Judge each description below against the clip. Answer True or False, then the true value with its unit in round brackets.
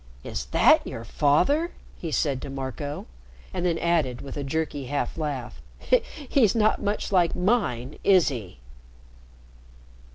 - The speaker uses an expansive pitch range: True (5.8 semitones)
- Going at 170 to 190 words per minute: False (135 wpm)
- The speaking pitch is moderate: True (150 Hz)